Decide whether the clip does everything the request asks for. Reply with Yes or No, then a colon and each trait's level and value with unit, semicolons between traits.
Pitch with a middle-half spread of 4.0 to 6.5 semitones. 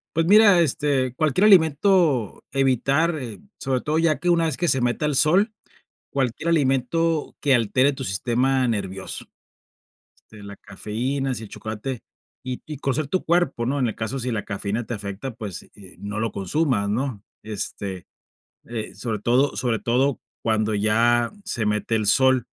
Yes: average, 5.1 semitones